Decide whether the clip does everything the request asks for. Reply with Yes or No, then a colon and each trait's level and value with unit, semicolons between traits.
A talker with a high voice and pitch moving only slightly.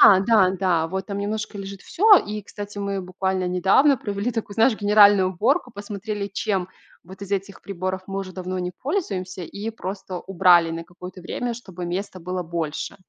Yes: high, 195 Hz; narrow, 2.1 semitones